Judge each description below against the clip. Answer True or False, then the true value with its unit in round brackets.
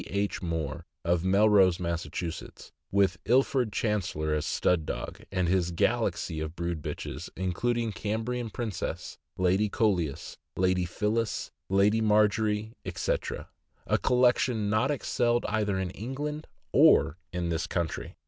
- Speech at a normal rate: False (125 wpm)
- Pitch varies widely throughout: False (4.2 semitones)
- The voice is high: False (100 Hz)